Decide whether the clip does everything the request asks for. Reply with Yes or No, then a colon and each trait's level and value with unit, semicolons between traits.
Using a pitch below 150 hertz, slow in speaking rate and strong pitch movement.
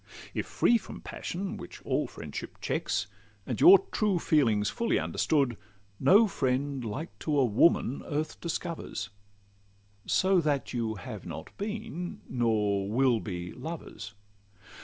Yes: medium, 140 Hz; slow, 130 wpm; wide, 7.6 semitones